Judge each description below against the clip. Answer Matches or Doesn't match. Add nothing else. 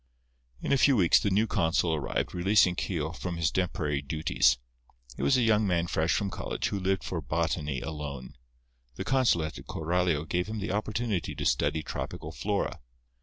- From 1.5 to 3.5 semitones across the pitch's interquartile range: Doesn't match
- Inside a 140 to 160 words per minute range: Doesn't match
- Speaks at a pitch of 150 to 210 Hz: Doesn't match